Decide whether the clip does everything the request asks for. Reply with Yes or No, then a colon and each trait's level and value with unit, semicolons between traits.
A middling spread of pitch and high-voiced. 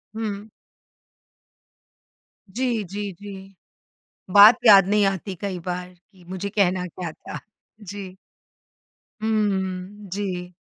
No: narrow, 2.0 semitones; high, 195 Hz